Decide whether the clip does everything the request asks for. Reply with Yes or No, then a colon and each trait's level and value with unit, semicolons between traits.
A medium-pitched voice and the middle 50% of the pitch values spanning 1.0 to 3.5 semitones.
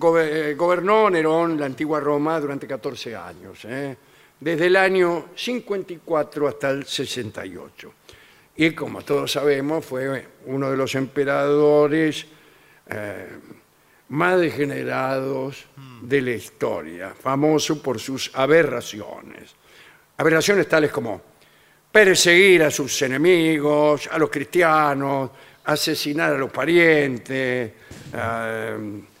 Yes: medium, 145 Hz; average, 3.2 semitones